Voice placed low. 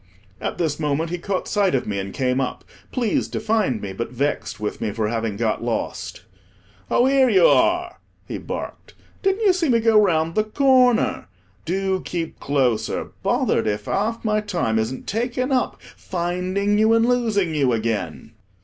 No: medium, 180 Hz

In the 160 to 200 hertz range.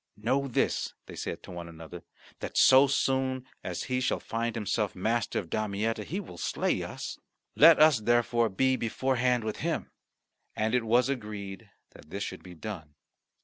No: low, 115 Hz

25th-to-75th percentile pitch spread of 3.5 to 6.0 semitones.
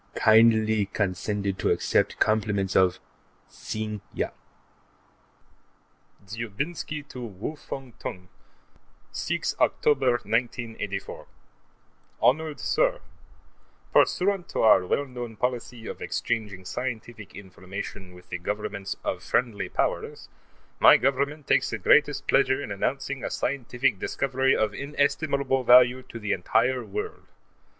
Yes: average, 4.8 semitones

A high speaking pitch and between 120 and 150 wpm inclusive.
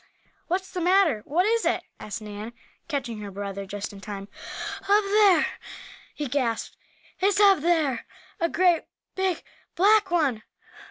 Yes: very high, 320 Hz; average, 145 wpm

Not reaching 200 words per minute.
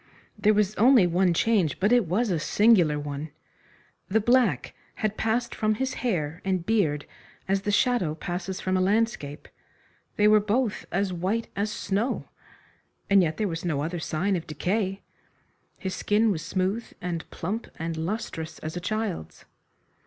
Yes: average, 160 wpm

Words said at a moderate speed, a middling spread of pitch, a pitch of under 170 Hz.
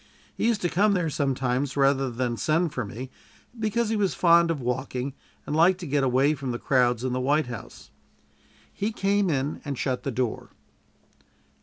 Yes: average, 185 wpm; average, 5.0 semitones; medium, 140 Hz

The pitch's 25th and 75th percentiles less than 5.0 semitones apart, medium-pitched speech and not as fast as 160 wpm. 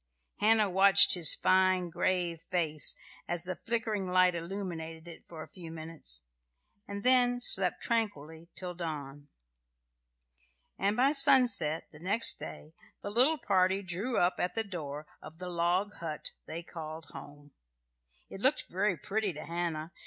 Yes: average, 3.8 semitones; medium, 180 Hz; average, 145 wpm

